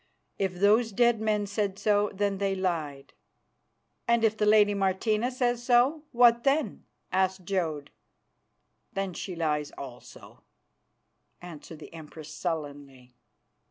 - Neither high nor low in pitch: No, high, 195 Hz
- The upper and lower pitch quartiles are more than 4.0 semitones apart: Yes, average, 5.2 semitones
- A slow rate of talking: Yes, slow, 125 wpm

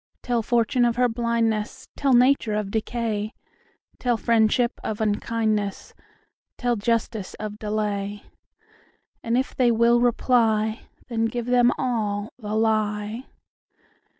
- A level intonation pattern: Yes, narrow, 2.1 semitones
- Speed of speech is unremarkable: No, slow, 95 wpm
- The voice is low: No, high, 225 Hz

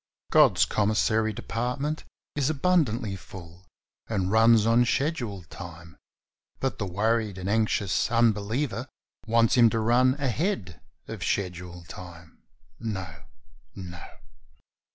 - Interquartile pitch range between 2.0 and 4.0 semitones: No, average, 4.7 semitones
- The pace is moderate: No, slow, 110 wpm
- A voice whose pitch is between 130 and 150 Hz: No, low, 110 Hz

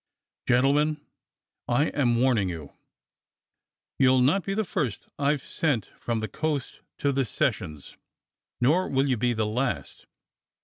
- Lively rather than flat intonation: No, average, 4.0 semitones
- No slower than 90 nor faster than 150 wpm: Yes, slow, 135 wpm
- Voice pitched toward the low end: Yes, low, 130 Hz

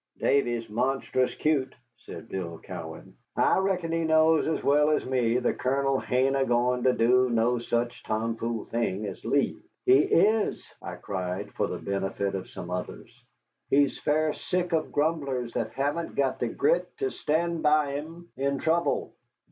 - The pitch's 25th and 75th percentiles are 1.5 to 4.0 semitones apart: No, average, 5.0 semitones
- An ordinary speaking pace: Yes, average, 165 wpm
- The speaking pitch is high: No, low, 135 Hz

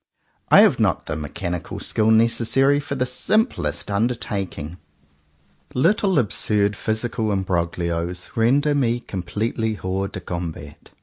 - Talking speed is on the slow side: Yes, slow, 115 wpm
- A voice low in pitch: Yes, low, 105 Hz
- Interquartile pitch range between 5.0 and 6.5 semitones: Yes, wide, 5.5 semitones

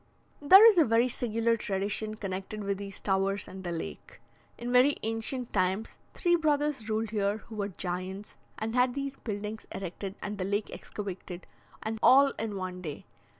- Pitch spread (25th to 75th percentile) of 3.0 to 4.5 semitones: Yes, average, 3.8 semitones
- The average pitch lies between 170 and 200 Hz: No, high, 215 Hz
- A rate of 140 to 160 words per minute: No, average, 170 wpm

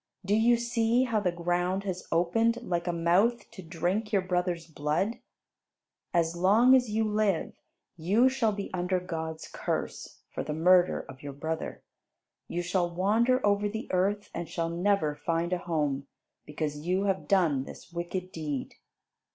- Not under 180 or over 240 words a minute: No, average, 160 wpm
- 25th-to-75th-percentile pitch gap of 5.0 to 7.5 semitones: No, average, 3.8 semitones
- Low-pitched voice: No, medium, 180 Hz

